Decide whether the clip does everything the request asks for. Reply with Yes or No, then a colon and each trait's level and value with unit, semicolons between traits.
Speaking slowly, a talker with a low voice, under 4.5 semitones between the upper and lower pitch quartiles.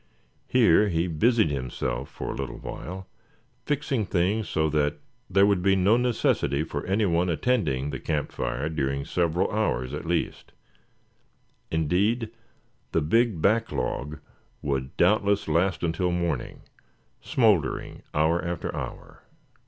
No: slow, 130 wpm; very low, 85 Hz; wide, 5.5 semitones